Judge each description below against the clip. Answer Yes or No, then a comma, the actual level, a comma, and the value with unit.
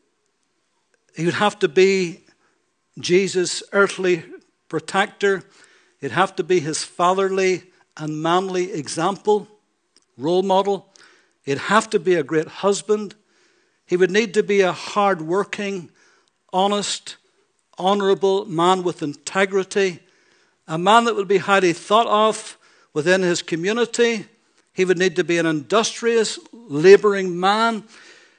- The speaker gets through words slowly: Yes, slow, 125 wpm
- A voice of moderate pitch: No, high, 195 Hz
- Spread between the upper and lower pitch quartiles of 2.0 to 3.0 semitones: Yes, average, 2.7 semitones